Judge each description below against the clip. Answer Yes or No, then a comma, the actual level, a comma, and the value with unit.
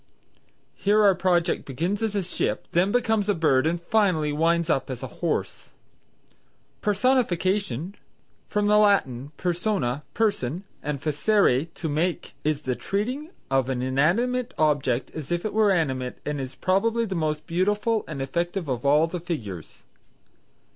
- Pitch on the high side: No, medium, 170 Hz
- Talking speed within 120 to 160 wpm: Yes, average, 150 wpm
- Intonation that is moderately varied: No, wide, 6.1 semitones